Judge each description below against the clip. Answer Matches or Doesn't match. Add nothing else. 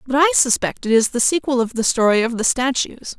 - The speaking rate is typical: Doesn't match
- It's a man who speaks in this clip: Doesn't match